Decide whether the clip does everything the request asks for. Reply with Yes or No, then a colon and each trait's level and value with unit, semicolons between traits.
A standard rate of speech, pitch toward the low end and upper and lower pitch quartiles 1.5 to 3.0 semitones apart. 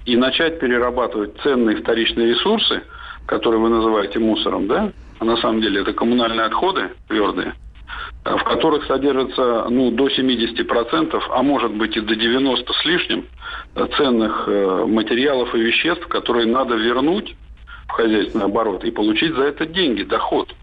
Yes: average, 140 wpm; low, 120 Hz; narrow, 2.6 semitones